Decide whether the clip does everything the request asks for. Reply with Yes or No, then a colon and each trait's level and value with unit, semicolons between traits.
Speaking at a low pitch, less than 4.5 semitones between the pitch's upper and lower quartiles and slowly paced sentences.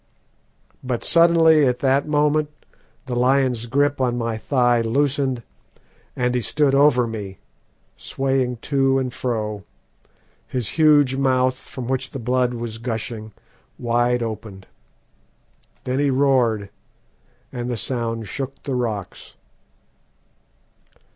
Yes: low, 125 Hz; narrow, 2.6 semitones; slow, 115 wpm